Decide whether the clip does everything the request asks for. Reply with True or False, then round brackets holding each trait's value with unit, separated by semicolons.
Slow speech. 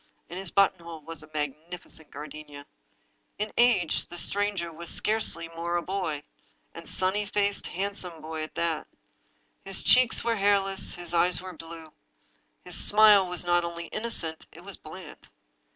False (170 wpm)